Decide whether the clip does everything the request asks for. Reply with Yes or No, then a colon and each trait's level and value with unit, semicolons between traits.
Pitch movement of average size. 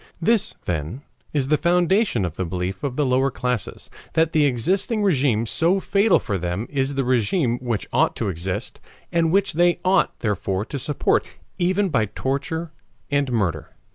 No: wide, 7.9 semitones